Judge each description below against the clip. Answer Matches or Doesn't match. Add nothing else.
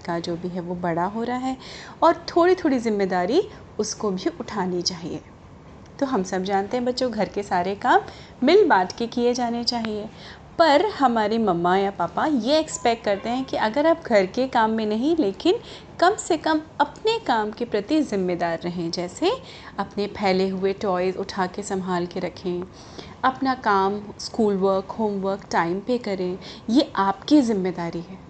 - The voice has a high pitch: Matches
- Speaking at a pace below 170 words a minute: Doesn't match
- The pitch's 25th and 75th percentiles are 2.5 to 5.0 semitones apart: Doesn't match